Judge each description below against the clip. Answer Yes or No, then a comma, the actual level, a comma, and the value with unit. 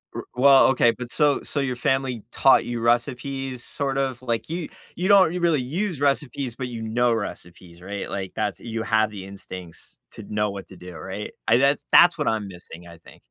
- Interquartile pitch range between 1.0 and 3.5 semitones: No, average, 5.0 semitones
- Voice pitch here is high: No, low, 120 Hz